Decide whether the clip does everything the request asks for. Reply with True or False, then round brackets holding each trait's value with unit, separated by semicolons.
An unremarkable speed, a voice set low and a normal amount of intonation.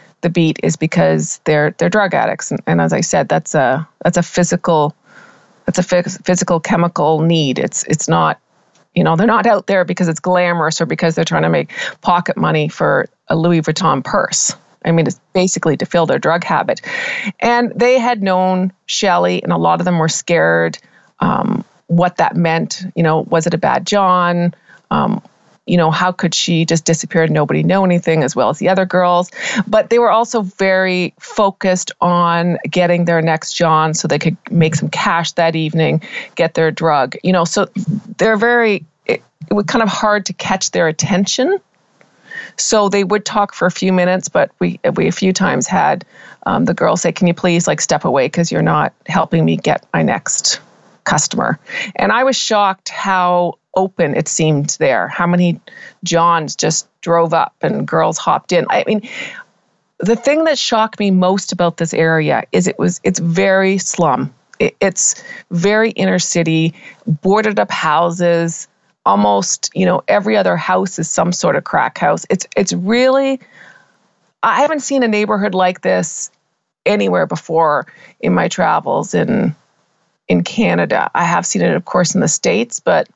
False (185 wpm; 175 Hz; 3.4 semitones)